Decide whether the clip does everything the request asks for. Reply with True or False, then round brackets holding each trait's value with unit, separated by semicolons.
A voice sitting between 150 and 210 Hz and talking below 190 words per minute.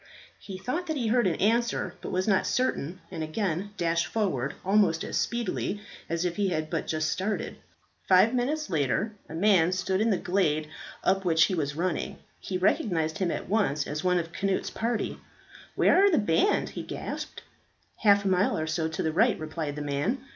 False (185 Hz; 195 wpm)